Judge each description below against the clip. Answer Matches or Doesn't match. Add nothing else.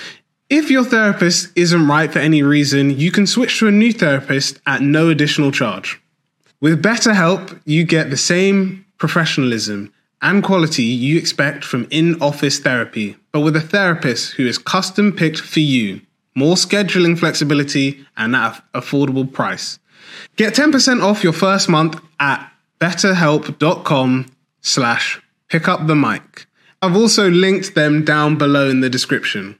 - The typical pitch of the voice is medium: Matches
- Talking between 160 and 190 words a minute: Doesn't match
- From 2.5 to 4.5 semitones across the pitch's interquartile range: Doesn't match